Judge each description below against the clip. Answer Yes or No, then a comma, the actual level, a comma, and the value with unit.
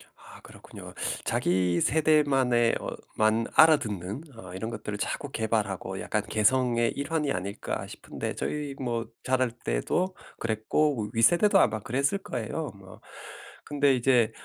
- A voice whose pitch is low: Yes, low, 120 Hz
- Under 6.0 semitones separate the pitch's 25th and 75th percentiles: Yes, average, 5.1 semitones